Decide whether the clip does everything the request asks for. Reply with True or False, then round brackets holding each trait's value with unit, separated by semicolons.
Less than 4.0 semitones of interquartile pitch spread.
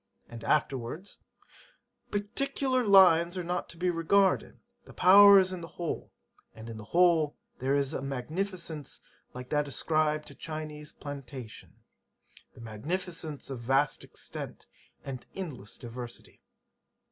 False (5.2 semitones)